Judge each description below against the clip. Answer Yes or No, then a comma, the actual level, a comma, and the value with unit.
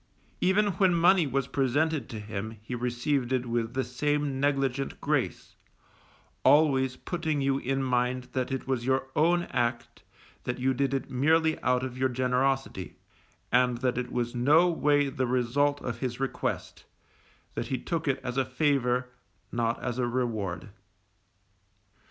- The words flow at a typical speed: Yes, average, 155 wpm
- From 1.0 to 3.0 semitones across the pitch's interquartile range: Yes, average, 2.7 semitones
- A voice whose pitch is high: No, low, 130 Hz